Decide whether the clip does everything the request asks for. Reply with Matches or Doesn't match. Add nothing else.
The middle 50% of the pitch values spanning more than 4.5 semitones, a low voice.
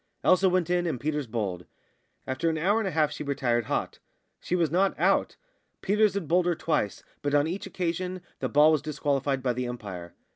Doesn't match